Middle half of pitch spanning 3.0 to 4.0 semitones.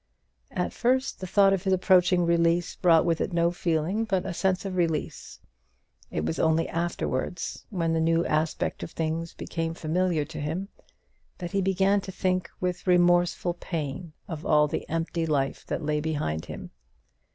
No: narrow, 2.4 semitones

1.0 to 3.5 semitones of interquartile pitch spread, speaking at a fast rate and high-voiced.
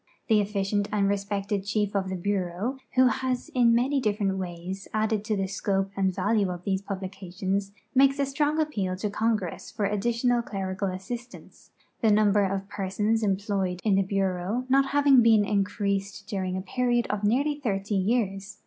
No: average, 3.0 semitones; average, 175 wpm; high, 205 Hz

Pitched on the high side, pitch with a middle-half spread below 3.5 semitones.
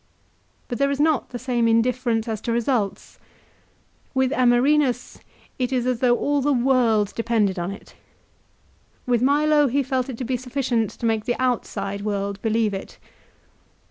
Yes: high, 245 Hz; average, 2.8 semitones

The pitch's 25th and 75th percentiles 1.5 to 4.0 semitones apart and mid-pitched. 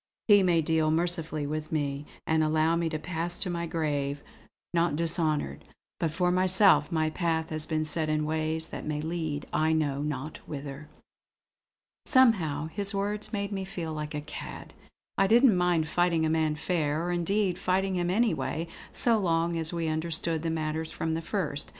Yes: narrow, 2.4 semitones; medium, 160 Hz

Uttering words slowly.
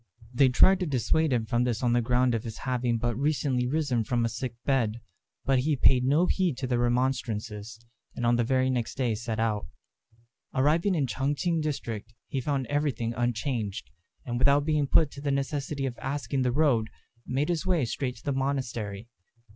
No: average, 195 wpm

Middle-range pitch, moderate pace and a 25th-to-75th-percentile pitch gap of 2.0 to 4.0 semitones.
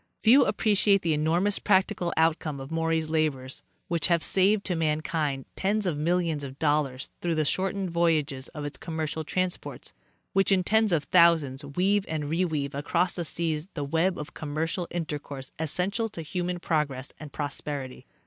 Yes: medium, 160 Hz; average, 165 wpm; average, 3.5 semitones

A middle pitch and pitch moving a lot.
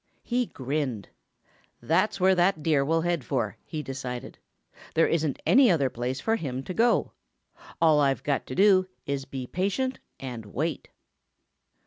Yes: medium, 150 Hz; wide, 5.8 semitones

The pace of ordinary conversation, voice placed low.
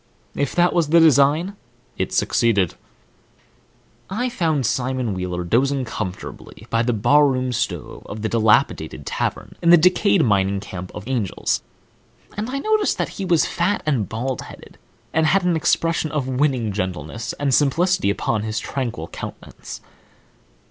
Yes: average, 155 wpm; low, 130 Hz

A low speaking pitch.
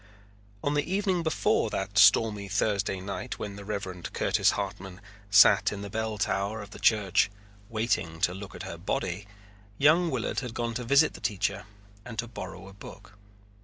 Yes: low, 105 Hz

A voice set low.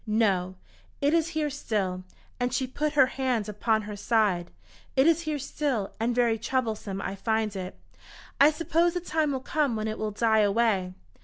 No: high, 230 Hz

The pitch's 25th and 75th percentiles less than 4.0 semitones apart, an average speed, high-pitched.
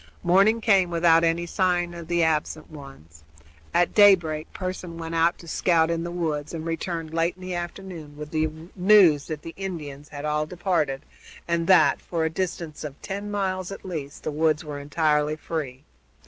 No: average, 2.8 semitones; average, 180 wpm; medium, 165 Hz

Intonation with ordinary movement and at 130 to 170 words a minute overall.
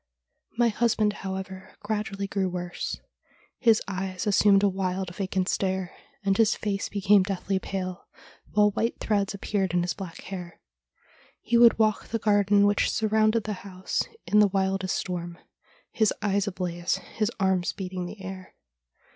No: narrow, 1.9 semitones; average, 150 wpm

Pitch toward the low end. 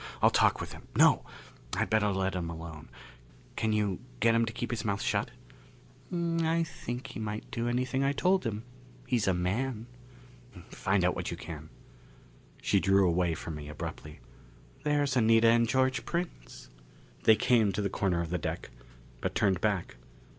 Yes: low, 110 Hz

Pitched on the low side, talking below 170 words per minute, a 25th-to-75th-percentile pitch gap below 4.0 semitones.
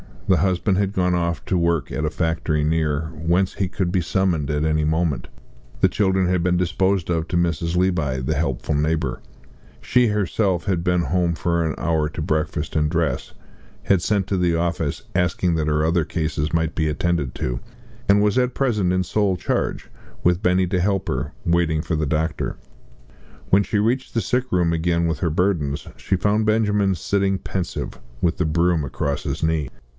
No: very low, 85 Hz; average, 190 wpm; average, 3.2 semitones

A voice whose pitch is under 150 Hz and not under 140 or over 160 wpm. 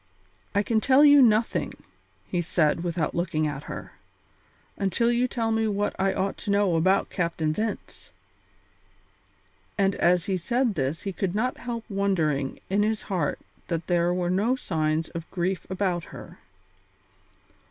No: high, 190 Hz; average, 150 wpm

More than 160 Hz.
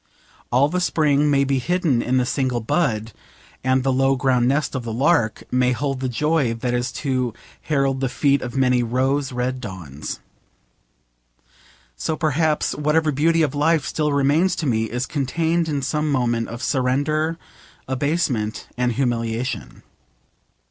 No: low, 135 Hz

